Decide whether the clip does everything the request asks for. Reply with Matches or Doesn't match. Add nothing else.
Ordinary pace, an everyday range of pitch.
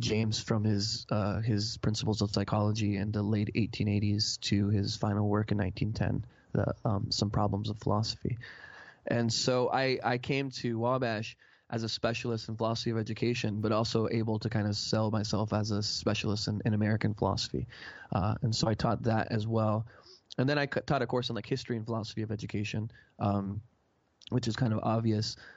Doesn't match